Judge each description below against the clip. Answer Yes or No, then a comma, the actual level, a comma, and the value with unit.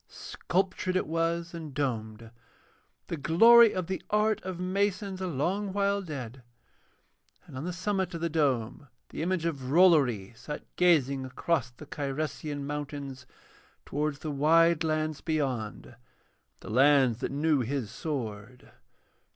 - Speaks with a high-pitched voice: No, medium, 155 Hz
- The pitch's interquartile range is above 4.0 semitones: Yes, average, 5.0 semitones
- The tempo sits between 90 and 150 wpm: Yes, slow, 135 wpm